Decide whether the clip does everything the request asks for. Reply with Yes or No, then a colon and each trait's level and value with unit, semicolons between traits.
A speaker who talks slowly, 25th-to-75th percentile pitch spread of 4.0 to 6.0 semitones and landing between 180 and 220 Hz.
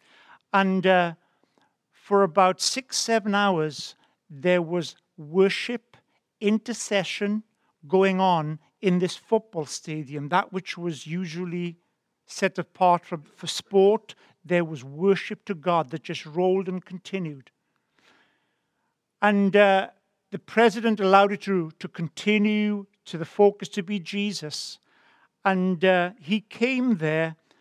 No: slow, 120 wpm; average, 3.0 semitones; high, 190 Hz